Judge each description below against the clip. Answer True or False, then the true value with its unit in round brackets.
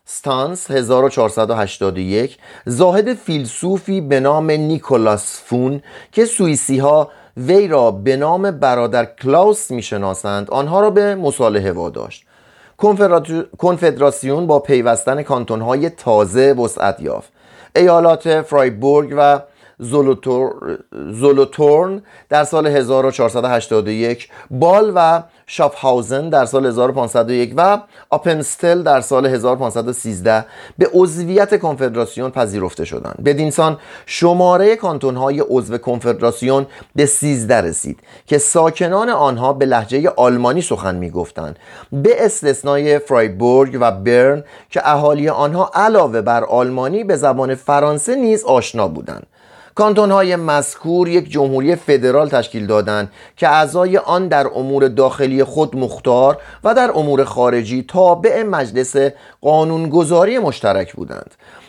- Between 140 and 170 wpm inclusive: False (115 wpm)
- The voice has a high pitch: False (140 Hz)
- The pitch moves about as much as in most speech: True (4.9 semitones)